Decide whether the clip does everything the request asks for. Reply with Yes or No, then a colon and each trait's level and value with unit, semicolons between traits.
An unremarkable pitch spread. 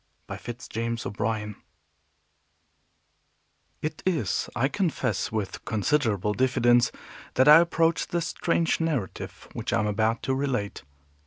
No: wide, 6.0 semitones